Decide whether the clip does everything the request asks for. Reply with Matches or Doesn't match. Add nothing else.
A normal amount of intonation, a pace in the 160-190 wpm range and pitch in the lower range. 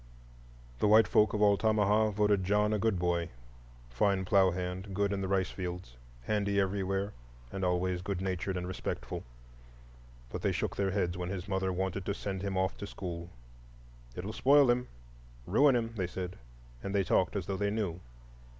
Doesn't match